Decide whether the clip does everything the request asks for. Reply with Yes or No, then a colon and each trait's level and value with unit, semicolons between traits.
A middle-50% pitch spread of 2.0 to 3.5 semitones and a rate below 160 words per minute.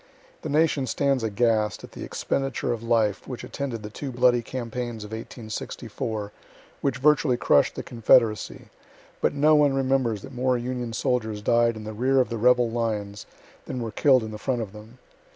No: average, 2.9 semitones; average, 180 wpm